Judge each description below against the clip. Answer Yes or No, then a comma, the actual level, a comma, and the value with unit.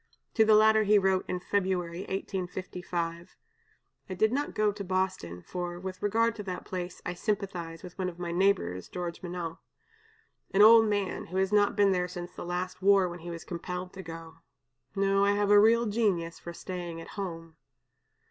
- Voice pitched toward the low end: No, medium, 185 Hz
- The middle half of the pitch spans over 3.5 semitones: No, narrow, 2.6 semitones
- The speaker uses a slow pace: No, average, 185 wpm